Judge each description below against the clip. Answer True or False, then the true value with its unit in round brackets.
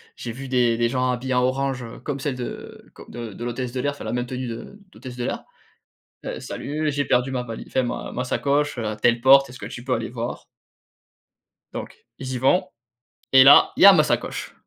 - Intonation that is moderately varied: False (2.2 semitones)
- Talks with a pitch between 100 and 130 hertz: True (125 Hz)